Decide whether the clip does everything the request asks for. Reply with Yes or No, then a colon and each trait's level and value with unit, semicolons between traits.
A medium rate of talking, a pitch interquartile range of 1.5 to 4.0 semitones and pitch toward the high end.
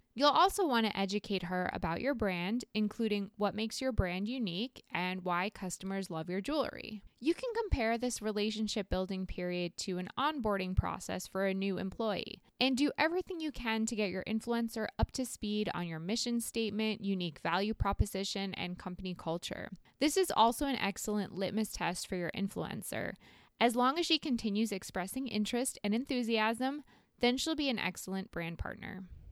No: average, 170 wpm; average, 4.4 semitones; high, 210 Hz